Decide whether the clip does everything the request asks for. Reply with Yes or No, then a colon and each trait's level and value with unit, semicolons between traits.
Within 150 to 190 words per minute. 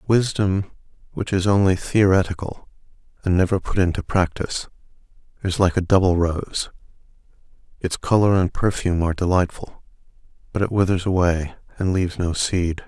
No: slow, 135 wpm